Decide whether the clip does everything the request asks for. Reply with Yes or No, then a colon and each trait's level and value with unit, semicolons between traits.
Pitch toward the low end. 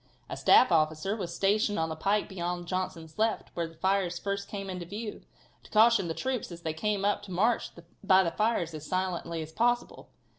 No: high, 190 Hz